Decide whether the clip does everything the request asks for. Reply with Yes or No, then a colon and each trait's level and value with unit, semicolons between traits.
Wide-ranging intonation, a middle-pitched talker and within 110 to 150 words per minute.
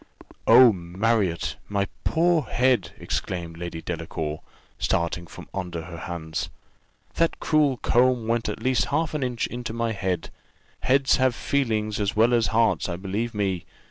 No: wide, 5.7 semitones; low, 110 Hz; average, 145 wpm